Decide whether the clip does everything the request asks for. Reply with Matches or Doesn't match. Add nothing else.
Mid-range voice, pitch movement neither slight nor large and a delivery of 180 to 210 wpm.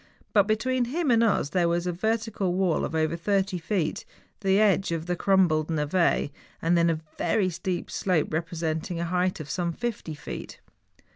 Matches